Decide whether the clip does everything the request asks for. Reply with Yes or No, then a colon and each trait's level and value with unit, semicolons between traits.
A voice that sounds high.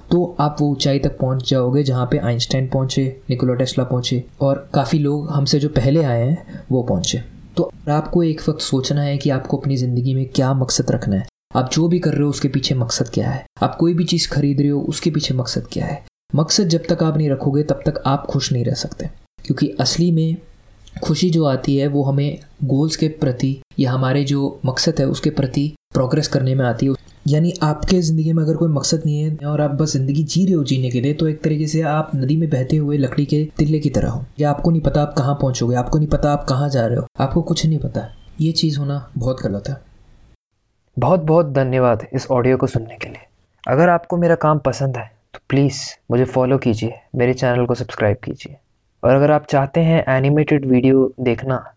No: medium, 140 Hz